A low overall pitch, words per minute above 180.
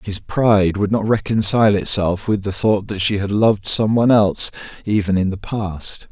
Yes: low, 100 Hz; average, 195 wpm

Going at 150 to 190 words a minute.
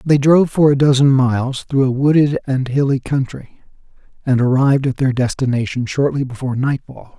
Yes: average, 165 wpm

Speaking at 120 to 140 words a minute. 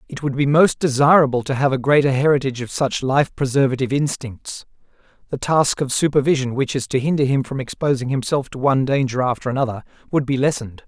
No: average, 195 wpm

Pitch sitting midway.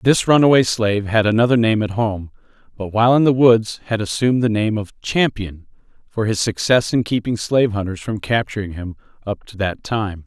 No: low, 110 Hz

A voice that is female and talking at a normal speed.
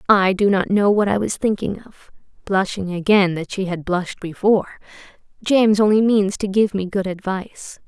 Yes: female; average, 185 wpm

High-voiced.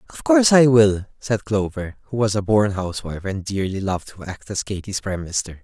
No: low, 105 Hz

